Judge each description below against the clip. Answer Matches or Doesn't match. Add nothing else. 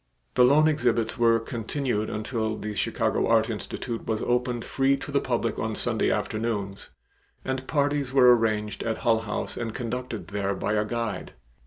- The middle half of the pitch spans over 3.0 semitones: Doesn't match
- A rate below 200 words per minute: Matches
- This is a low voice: Matches